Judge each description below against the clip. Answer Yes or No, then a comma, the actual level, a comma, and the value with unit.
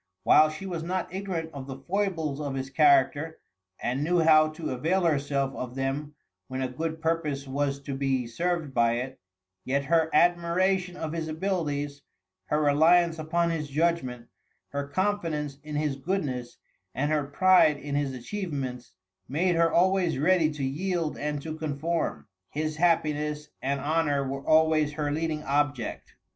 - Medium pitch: Yes, medium, 150 Hz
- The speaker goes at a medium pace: Yes, average, 155 wpm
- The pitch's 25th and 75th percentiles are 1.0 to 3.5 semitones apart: Yes, average, 3.1 semitones